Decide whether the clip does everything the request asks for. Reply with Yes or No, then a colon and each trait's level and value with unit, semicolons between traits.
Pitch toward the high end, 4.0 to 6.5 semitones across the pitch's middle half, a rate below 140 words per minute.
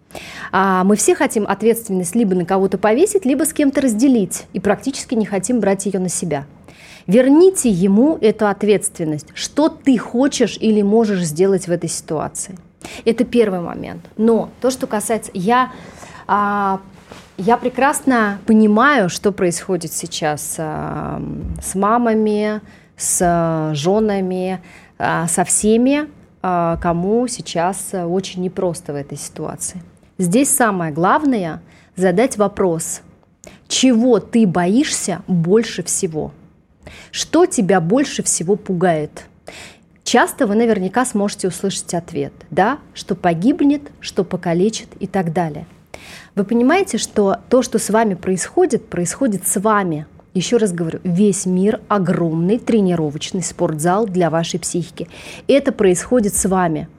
Yes: high, 200 Hz; average, 4.4 semitones; average, 120 wpm